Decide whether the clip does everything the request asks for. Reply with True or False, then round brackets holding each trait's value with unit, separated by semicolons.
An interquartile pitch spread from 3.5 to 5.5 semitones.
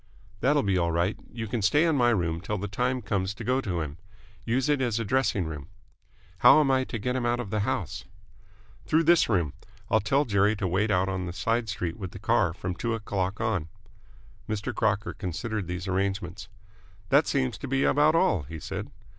True (4.9 semitones)